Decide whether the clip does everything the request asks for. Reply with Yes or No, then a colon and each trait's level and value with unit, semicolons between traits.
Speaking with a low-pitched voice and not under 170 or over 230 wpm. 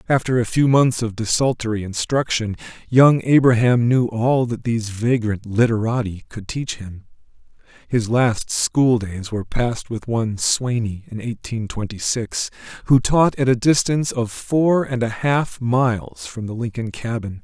No: low, 115 Hz; average, 160 wpm